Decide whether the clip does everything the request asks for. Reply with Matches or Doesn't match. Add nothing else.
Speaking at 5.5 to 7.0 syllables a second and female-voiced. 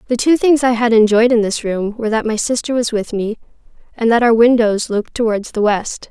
Matches